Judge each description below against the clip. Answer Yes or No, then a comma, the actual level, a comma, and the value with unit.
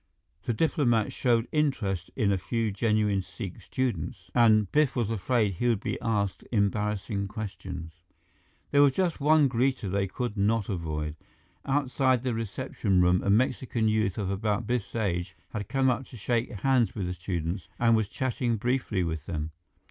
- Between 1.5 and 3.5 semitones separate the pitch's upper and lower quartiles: No, average, 4.2 semitones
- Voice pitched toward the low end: Yes, low, 110 Hz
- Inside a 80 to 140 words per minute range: No, average, 165 wpm